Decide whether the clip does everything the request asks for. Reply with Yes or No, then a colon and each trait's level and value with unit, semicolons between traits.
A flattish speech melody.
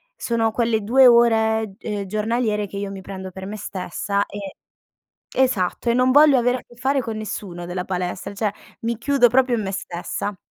No: average, 3.5 semitones